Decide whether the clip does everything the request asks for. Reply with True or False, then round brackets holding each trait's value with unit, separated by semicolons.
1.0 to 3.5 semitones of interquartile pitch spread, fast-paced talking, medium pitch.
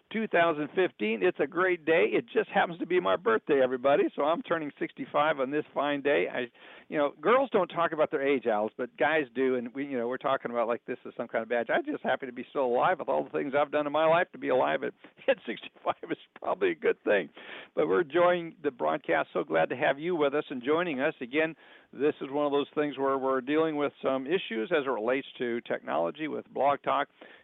False (4.1 semitones; 245 wpm; 145 Hz)